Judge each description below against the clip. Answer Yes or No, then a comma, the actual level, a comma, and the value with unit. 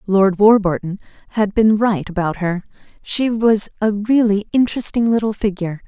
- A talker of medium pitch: No, high, 205 Hz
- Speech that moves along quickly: No, average, 145 wpm